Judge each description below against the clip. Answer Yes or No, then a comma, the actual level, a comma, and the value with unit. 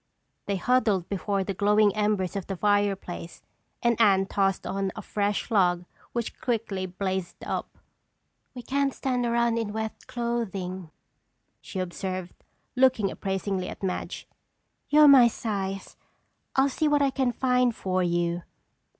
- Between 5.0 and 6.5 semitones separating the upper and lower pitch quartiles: No, average, 3.9 semitones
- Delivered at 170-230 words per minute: No, average, 140 wpm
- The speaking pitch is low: No, high, 205 Hz